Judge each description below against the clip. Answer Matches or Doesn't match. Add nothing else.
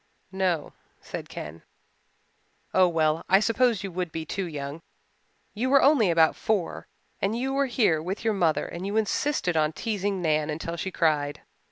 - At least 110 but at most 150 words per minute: Doesn't match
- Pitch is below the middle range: Doesn't match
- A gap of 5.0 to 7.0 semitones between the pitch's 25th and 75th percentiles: Matches